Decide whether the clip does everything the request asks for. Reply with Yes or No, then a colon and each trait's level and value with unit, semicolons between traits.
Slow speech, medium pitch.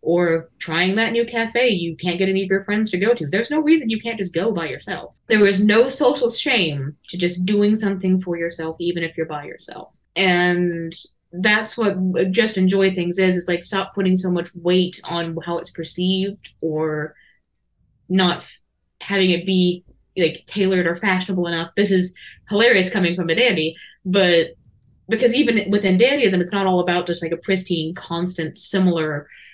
No: average, 185 wpm; medium, 180 Hz